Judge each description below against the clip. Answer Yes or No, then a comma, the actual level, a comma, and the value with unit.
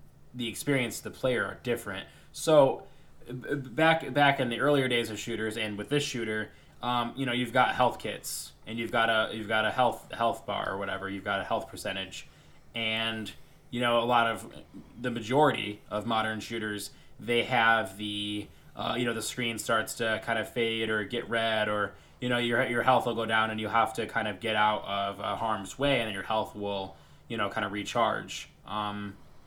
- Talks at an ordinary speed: No, fast, 210 wpm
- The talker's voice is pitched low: Yes, low, 110 Hz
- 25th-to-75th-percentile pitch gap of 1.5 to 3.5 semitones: Yes, narrow, 2.5 semitones